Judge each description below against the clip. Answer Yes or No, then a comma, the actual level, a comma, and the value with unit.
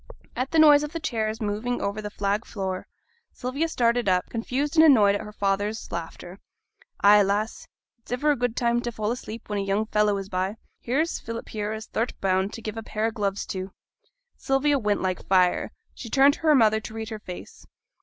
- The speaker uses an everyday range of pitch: Yes, average, 3.4 semitones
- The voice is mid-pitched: No, high, 220 Hz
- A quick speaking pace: Yes, fast, 210 wpm